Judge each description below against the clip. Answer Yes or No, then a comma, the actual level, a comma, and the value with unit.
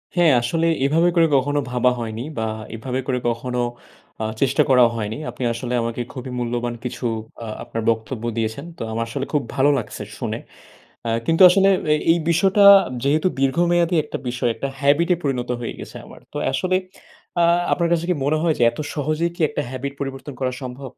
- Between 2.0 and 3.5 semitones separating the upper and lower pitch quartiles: No, average, 4.7 semitones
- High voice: No, low, 135 Hz